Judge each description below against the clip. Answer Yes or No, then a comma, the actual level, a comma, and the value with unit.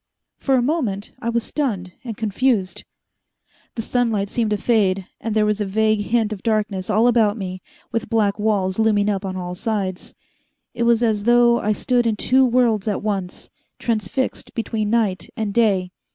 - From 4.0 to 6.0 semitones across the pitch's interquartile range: No, average, 2.8 semitones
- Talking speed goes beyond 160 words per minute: Yes, average, 180 wpm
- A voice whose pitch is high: Yes, high, 215 Hz